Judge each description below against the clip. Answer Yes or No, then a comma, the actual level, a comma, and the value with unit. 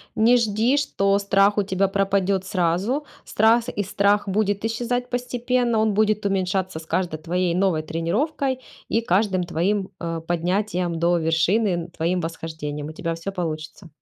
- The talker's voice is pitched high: Yes, high, 195 Hz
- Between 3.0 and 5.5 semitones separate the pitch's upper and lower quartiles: Yes, average, 4.1 semitones